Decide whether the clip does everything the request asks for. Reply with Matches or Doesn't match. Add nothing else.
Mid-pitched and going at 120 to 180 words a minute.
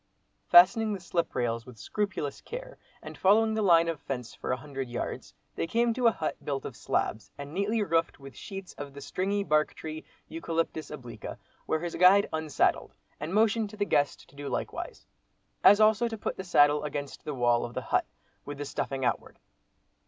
Doesn't match